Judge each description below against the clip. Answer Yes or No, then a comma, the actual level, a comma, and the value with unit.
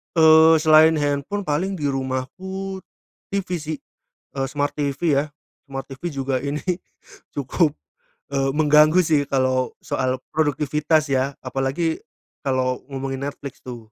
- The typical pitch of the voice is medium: Yes, medium, 145 Hz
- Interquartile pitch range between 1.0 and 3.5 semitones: Yes, average, 2.9 semitones